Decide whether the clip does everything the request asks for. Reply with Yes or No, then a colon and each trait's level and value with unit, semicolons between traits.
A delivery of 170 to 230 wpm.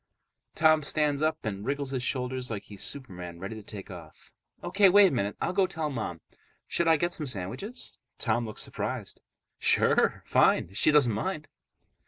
Yes: average, 180 wpm